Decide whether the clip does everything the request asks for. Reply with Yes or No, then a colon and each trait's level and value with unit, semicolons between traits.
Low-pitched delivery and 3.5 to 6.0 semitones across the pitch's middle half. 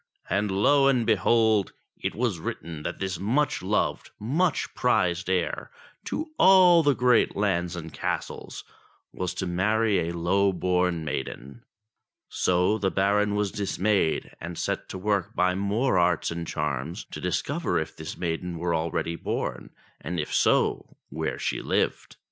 Yes: very low, 95 Hz; average, 4.0 semitones